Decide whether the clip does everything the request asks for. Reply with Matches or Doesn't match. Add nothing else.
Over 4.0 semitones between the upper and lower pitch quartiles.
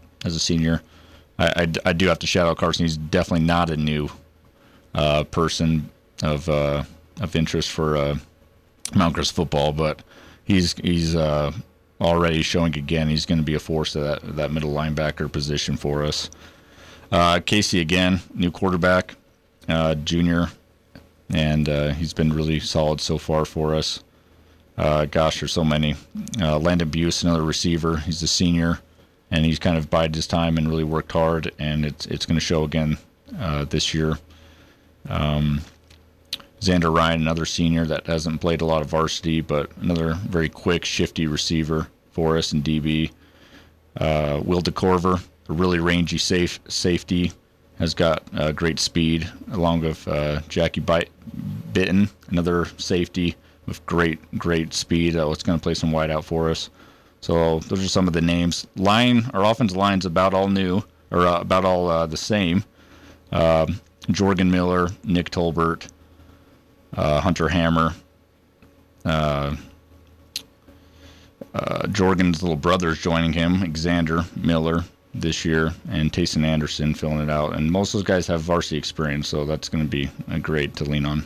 Doesn't match